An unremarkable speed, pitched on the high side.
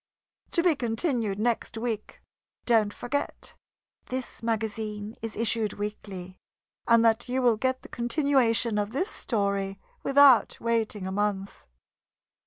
No: slow, 125 wpm; high, 225 Hz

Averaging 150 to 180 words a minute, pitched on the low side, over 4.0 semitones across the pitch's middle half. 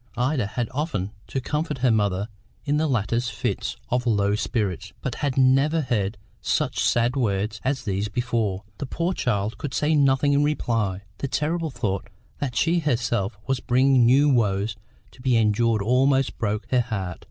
Yes: average, 170 wpm; low, 120 Hz; average, 4.5 semitones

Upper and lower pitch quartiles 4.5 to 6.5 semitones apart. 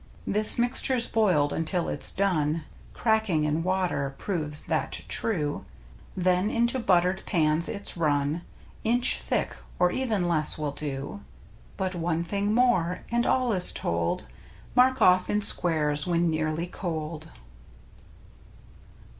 Yes: average, 5.2 semitones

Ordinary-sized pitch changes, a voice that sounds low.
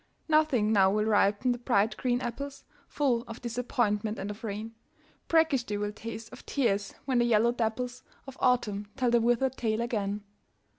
No: average, 3.0 semitones; high, 235 Hz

